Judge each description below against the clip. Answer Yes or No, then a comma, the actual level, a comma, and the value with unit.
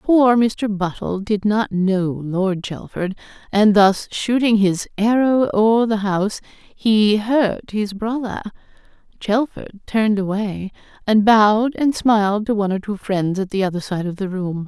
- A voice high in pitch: Yes, high, 205 Hz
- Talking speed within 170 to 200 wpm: No, average, 160 wpm